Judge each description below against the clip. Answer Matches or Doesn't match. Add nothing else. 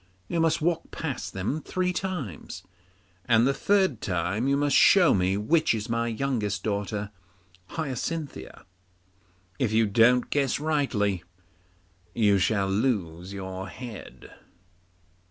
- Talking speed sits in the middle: Doesn't match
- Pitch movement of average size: Doesn't match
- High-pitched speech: Doesn't match